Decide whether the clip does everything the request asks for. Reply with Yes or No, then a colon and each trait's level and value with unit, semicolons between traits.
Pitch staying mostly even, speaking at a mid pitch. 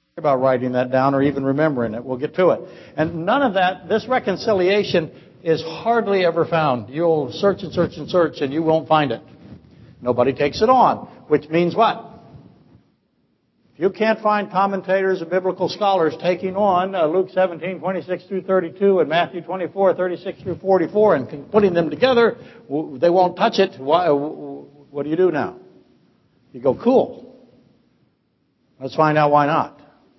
No: average, 4.1 semitones; medium, 175 Hz